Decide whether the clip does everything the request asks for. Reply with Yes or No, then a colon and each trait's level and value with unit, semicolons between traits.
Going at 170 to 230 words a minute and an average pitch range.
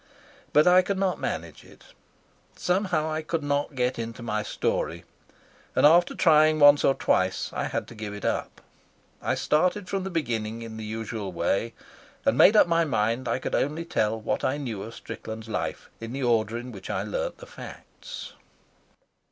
No: average, 185 wpm; wide, 6.2 semitones